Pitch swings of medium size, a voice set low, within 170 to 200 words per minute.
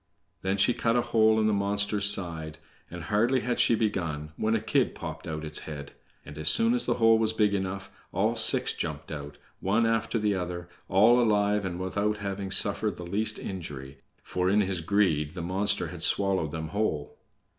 Yes: average, 4.1 semitones; low, 100 Hz; average, 195 wpm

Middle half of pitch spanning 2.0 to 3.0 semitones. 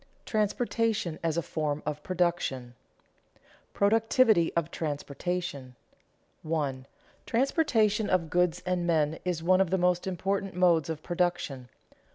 No: average, 3.6 semitones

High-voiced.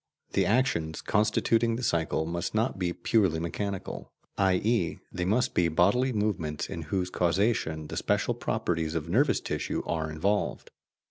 No: very low, 90 Hz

